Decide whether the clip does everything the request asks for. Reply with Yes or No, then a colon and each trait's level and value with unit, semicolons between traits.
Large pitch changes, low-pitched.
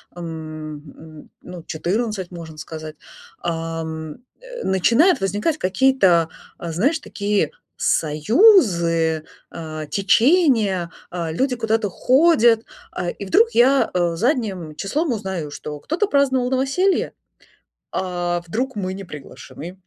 No: wide, 7.6 semitones; high, 190 Hz